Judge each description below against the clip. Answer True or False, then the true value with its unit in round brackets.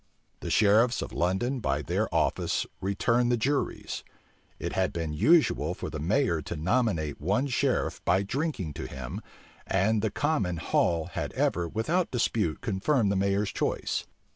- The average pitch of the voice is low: True (100 Hz)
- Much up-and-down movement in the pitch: True (6.2 semitones)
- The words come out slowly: False (155 wpm)